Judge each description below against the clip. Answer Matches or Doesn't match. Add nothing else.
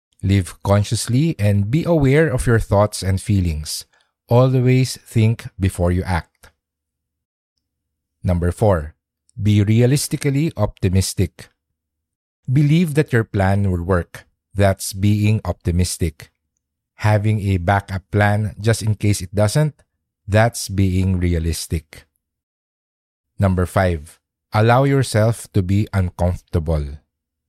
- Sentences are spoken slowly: Matches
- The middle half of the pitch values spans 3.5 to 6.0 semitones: Matches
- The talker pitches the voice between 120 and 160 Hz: Doesn't match